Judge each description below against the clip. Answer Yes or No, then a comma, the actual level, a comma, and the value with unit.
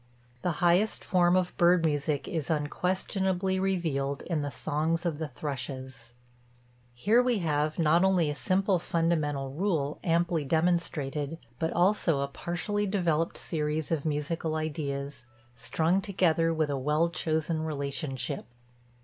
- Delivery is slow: Yes, slow, 130 wpm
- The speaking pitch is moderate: Yes, medium, 160 Hz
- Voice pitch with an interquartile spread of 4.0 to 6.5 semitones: No, average, 3.2 semitones